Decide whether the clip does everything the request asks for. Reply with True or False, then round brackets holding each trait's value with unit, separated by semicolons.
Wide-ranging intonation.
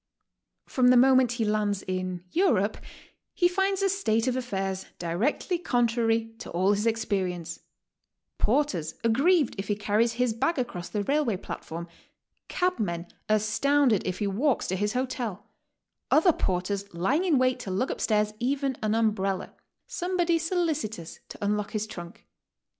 True (5.8 semitones)